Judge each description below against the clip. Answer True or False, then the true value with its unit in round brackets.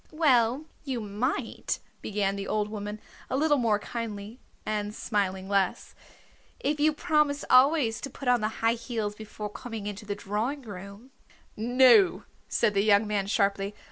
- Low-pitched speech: False (215 Hz)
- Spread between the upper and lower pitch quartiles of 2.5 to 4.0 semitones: True (3.7 semitones)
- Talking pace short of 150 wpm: False (160 wpm)